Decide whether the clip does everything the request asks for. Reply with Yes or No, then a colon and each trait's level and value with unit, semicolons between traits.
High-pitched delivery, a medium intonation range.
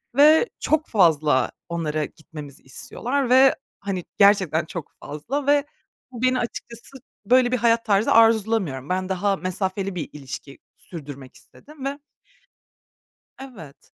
No: high, 200 Hz; wide, 8.2 semitones